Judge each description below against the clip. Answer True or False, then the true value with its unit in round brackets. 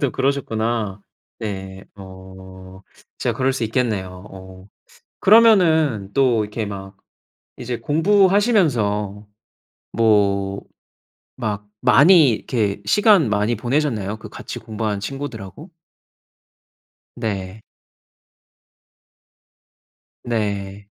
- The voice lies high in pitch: False (110 Hz)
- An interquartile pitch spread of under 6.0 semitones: True (5.5 semitones)